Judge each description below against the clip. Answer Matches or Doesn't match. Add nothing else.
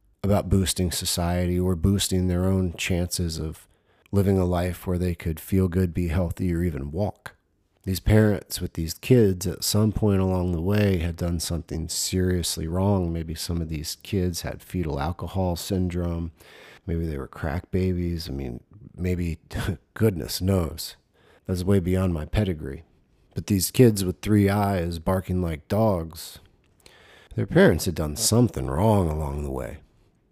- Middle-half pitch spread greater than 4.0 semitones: Doesn't match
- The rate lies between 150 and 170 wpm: Matches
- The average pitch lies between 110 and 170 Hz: Doesn't match